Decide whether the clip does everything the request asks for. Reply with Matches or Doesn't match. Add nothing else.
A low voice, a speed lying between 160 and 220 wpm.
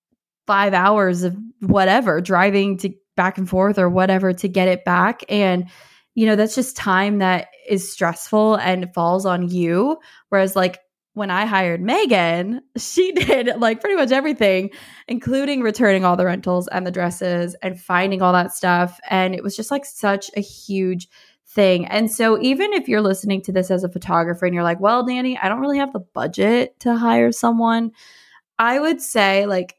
Doesn't match